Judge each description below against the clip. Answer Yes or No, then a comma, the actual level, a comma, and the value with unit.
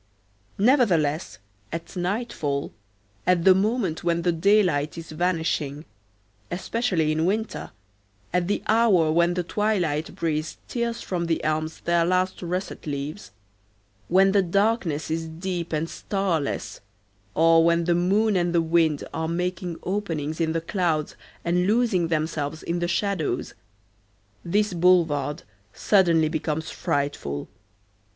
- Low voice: No, medium, 170 Hz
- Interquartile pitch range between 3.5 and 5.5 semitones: No, average, 3.0 semitones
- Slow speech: Yes, slow, 130 wpm